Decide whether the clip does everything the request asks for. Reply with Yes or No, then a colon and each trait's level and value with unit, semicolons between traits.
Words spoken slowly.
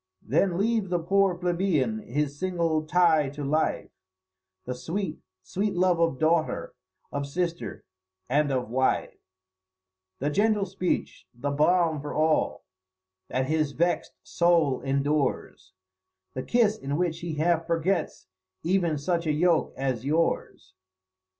Yes: slow, 130 wpm